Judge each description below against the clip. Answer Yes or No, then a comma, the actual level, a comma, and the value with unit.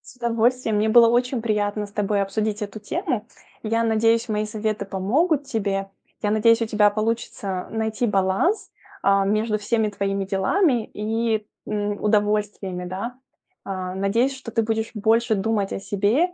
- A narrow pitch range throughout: Yes, narrow, 2.3 semitones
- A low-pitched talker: No, high, 215 Hz